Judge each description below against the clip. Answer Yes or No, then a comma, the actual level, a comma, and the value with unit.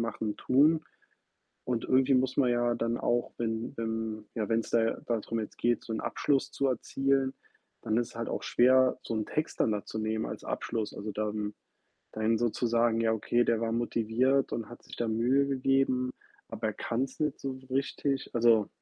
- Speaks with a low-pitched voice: Yes, low, 120 Hz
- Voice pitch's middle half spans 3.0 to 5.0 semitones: No, narrow, 2.6 semitones